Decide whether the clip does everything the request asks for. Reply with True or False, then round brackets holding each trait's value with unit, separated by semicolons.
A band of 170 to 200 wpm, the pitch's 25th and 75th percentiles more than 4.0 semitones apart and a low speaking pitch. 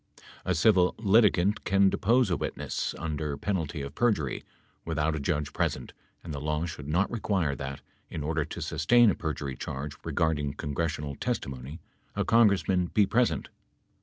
False (160 wpm; 4.9 semitones; 80 Hz)